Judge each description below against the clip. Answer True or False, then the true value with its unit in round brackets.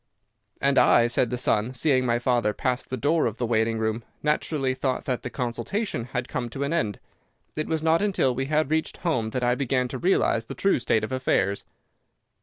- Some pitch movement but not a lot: True (4.0 semitones)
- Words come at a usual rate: False (210 wpm)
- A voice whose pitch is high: False (130 Hz)